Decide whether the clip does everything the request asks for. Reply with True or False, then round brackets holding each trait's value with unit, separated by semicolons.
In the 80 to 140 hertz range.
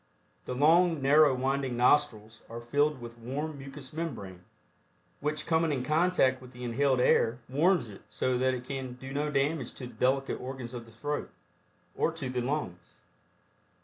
True (135 Hz)